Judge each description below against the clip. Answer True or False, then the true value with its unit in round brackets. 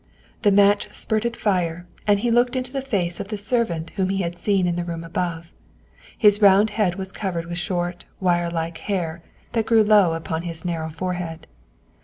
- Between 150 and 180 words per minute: False (190 wpm)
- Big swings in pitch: False (3.5 semitones)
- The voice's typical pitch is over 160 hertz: True (185 Hz)